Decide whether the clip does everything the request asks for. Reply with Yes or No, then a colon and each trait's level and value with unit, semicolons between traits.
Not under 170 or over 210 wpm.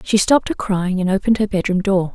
No: fast, 250 wpm